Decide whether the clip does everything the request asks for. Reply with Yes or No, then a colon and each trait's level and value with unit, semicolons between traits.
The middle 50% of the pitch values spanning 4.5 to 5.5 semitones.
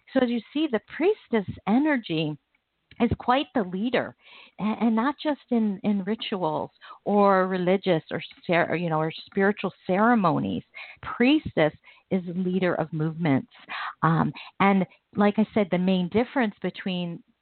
Yes: average, 4.8 semitones